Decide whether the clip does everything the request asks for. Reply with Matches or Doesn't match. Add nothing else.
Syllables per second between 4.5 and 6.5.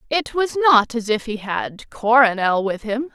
Doesn't match